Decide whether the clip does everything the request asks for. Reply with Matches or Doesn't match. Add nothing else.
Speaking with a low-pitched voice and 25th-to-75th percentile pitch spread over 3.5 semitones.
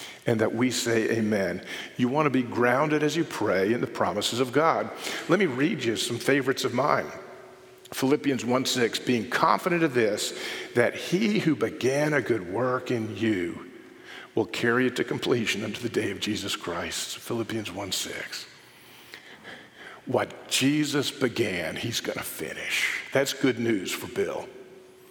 Matches